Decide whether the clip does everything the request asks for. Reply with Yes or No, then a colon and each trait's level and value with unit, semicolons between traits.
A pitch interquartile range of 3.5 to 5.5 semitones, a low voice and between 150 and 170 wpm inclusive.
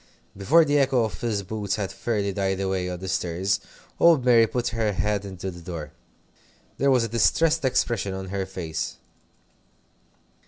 Yes: average, 3.9 semitones; low, 100 Hz; average, 165 wpm